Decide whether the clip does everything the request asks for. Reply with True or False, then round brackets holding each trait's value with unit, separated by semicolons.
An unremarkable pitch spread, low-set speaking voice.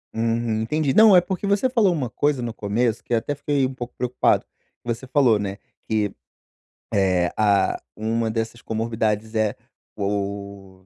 True (4.3 semitones; 115 Hz)